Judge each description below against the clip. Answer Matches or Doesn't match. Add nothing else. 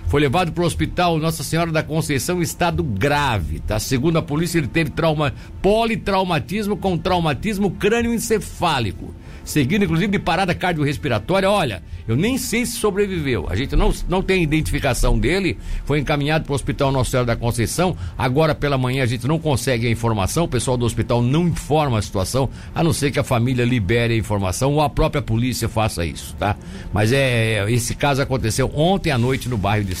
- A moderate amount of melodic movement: Doesn't match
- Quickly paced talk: Matches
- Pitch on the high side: Doesn't match